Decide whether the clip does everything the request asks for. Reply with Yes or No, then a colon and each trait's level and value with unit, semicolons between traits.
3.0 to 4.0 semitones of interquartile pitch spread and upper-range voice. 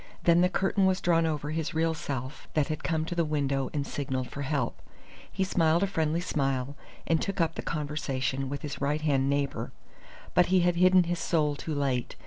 No: average, 3.4 semitones; medium, 155 Hz